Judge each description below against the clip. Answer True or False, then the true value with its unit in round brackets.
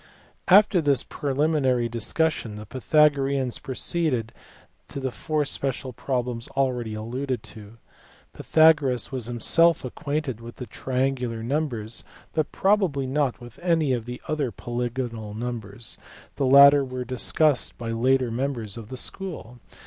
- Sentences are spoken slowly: True (125 wpm)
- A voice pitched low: True (130 Hz)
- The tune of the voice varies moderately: True (3.6 semitones)